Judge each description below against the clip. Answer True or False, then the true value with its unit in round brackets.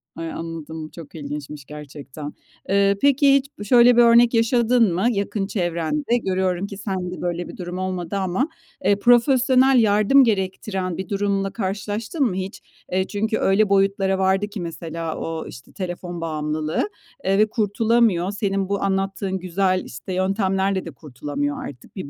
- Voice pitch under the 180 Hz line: False (195 Hz)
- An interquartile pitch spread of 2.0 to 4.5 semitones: True (3.6 semitones)